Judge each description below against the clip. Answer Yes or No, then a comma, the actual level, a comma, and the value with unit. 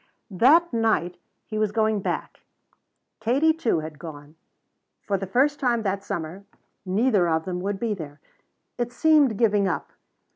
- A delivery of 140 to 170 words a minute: Yes, average, 150 wpm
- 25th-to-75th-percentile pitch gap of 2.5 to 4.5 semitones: No, average, 5.2 semitones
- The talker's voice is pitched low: No, high, 205 Hz